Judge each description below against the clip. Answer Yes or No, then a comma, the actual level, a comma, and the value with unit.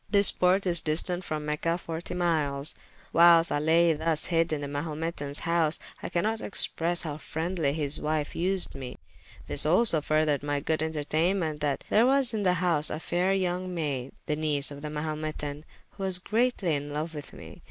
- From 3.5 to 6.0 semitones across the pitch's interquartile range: No, average, 3.0 semitones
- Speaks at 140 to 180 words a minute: No, average, 190 wpm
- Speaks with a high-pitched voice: No, medium, 160 Hz